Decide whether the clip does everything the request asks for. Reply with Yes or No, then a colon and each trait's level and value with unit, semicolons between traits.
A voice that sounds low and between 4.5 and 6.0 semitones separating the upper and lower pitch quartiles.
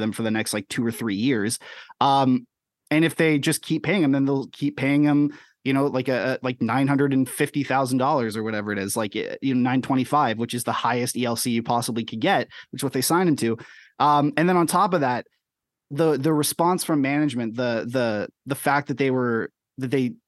No: low, 130 Hz; average, 3.6 semitones